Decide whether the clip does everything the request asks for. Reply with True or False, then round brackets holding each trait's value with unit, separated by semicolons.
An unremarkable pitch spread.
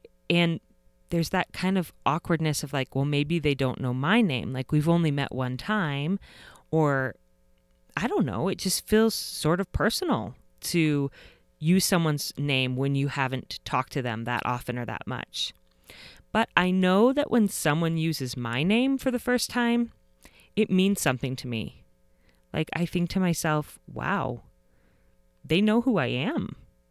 False (6.3 semitones)